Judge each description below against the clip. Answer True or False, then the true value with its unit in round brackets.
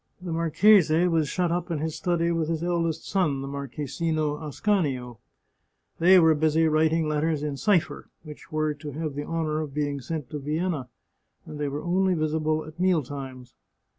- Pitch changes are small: True (2.3 semitones)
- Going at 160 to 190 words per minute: True (170 wpm)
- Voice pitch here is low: False (155 Hz)